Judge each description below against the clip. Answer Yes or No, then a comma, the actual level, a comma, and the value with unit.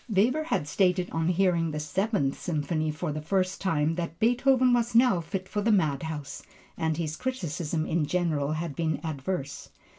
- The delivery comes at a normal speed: Yes, average, 170 wpm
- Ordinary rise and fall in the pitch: Yes, average, 4.1 semitones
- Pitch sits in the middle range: Yes, medium, 170 Hz